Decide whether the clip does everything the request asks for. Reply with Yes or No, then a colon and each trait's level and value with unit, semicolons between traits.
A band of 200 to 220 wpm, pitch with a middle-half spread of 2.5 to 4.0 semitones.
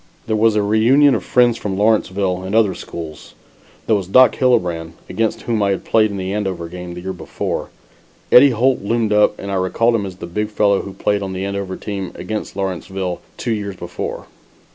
Yes: fast, 205 wpm; average, 2.9 semitones